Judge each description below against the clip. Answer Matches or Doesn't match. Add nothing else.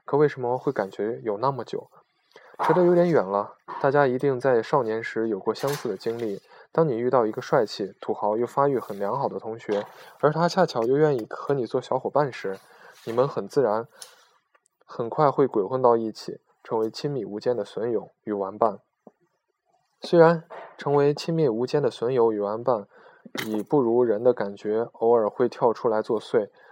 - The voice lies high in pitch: Doesn't match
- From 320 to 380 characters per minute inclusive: Doesn't match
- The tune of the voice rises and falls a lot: Matches